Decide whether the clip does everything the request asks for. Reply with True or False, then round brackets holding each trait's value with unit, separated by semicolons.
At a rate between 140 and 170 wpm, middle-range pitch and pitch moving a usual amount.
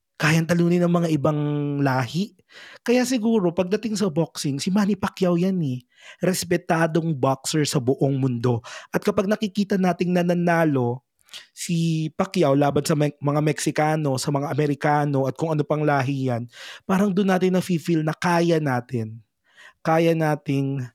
True (145 wpm; 160 Hz; 4.3 semitones)